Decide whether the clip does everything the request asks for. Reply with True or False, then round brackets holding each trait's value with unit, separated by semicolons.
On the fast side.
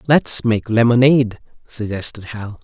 False (115 wpm)